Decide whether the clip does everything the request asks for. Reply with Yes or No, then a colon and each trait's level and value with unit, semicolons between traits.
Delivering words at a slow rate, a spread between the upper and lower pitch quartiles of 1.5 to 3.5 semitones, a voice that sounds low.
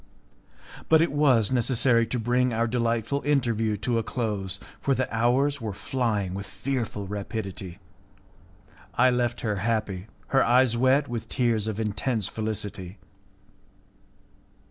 Yes: slow, 130 wpm; average, 3.2 semitones; low, 115 Hz